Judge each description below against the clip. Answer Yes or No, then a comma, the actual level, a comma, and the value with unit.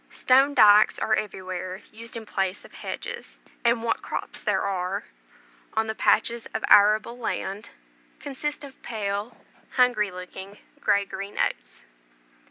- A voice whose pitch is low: No, high, 215 Hz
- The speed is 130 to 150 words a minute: Yes, slow, 135 wpm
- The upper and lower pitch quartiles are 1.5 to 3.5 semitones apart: Yes, average, 3.2 semitones